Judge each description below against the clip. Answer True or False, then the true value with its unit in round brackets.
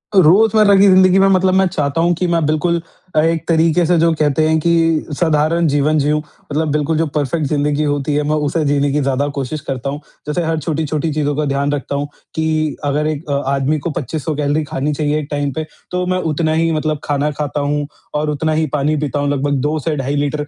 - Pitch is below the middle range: False (150 Hz)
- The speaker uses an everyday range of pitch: False (2.1 semitones)